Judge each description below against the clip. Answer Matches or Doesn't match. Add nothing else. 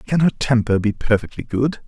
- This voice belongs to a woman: Doesn't match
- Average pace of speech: Matches